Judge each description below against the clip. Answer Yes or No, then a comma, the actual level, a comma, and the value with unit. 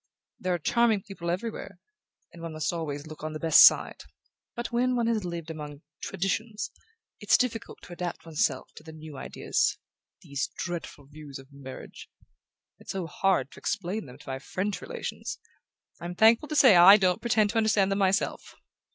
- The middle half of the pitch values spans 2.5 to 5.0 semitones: No, wide, 5.5 semitones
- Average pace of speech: Yes, average, 175 wpm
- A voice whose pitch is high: No, medium, 180 Hz